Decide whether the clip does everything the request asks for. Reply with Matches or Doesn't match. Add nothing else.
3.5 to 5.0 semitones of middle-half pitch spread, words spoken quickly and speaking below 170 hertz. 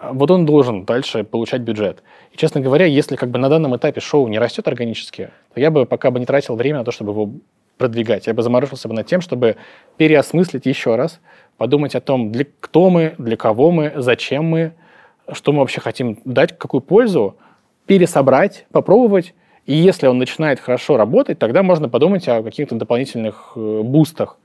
Matches